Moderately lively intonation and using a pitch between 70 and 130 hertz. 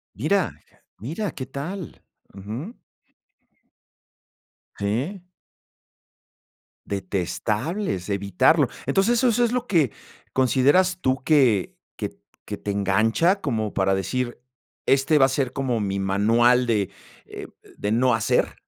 No: wide, 7.5 semitones; low, 125 Hz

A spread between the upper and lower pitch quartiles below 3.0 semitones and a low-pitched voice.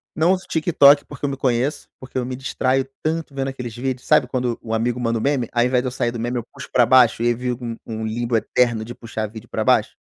Yes: narrow, 2.4 semitones; low, 125 Hz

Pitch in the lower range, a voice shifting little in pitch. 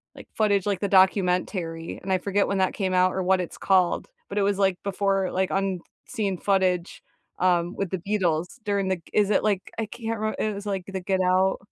No: high, 190 Hz; narrow, 1.6 semitones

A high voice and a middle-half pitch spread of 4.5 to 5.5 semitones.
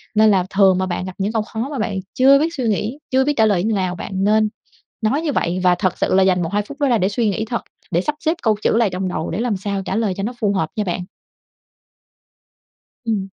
No: high, 210 Hz; average, 3.7 semitones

